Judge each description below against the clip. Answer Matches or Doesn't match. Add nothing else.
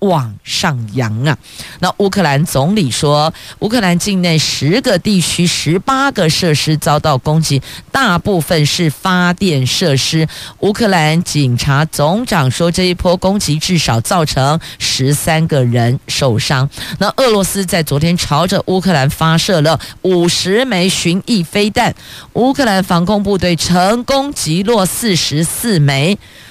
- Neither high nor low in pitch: Matches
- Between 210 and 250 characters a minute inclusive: Matches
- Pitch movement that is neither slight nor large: Matches